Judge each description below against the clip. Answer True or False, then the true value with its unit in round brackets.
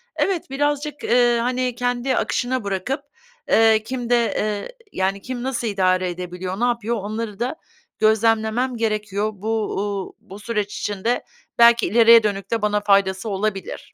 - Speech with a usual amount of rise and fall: True (3.3 semitones)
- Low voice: False (220 Hz)